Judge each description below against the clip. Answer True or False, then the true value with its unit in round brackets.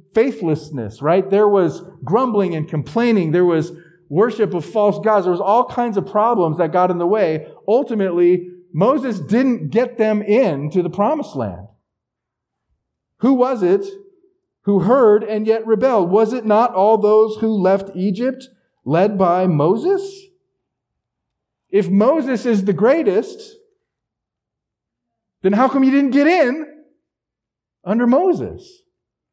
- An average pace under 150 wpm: True (135 wpm)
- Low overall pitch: False (210 Hz)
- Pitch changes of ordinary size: False (6.5 semitones)